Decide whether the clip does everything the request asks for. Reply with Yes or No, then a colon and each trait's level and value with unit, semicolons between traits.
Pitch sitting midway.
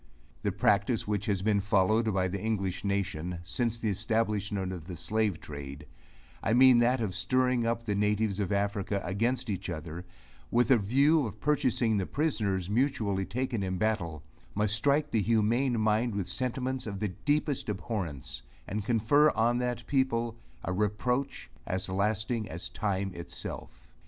No: low, 105 Hz